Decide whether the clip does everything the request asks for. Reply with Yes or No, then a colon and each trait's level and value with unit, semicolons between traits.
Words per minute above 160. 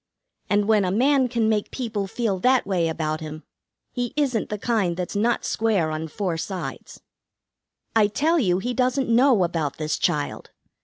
Yes: average, 170 wpm